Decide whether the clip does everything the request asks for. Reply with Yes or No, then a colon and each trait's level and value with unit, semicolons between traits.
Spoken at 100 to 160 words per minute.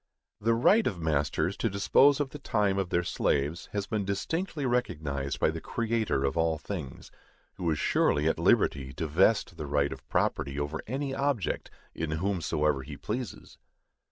No: average, 170 wpm